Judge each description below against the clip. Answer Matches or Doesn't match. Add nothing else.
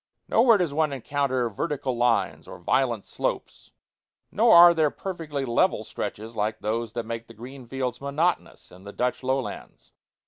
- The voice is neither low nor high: Doesn't match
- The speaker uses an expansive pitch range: Doesn't match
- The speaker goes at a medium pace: Matches